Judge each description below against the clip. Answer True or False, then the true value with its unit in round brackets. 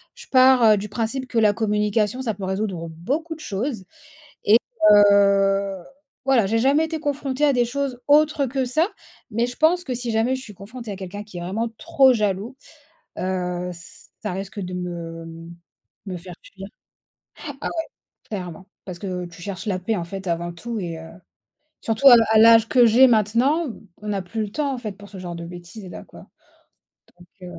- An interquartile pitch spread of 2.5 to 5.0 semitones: False (5.4 semitones)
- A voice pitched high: True (210 Hz)